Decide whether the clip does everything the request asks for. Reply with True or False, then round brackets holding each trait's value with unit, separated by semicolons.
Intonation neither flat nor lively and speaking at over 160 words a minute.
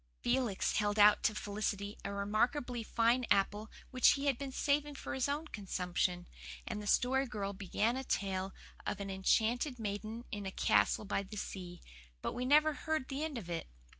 True (4.5 semitones; 185 wpm)